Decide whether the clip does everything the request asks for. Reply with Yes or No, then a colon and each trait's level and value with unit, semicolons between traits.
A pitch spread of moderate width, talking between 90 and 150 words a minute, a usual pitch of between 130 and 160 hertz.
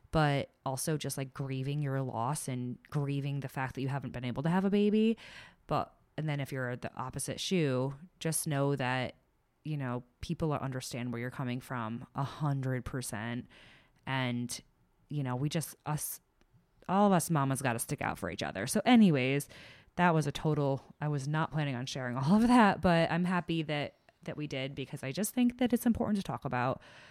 No: average, 3.8 semitones; average, 200 wpm; medium, 140 Hz